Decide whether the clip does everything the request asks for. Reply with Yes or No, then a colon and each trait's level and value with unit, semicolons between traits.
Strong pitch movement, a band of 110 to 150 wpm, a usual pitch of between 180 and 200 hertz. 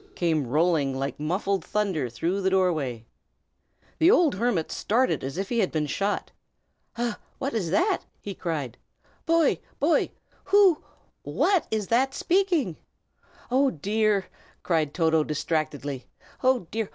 Yes: wide, 7.9 semitones; slow, 135 wpm; high, 190 Hz